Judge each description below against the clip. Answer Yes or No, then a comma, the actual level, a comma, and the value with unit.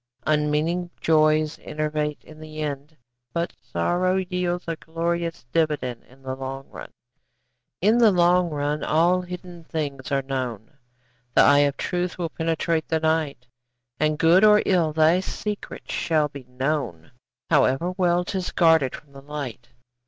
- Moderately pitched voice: Yes, medium, 155 Hz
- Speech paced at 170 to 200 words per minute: No, average, 145 wpm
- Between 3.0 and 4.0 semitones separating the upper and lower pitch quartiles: Yes, average, 3.4 semitones